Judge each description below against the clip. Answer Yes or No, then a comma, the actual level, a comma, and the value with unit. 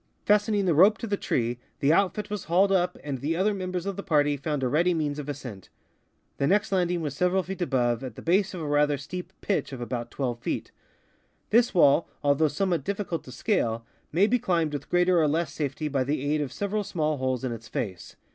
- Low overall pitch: No, medium, 160 Hz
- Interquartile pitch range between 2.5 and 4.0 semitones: No, wide, 5.4 semitones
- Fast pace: Yes, fast, 220 wpm